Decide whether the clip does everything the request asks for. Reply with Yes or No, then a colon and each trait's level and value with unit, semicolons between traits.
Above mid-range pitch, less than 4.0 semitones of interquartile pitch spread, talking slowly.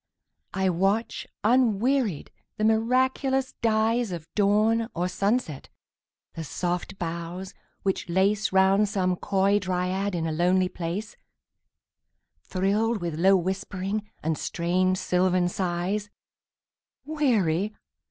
Yes: high, 195 Hz; average, 3.2 semitones; slow, 95 wpm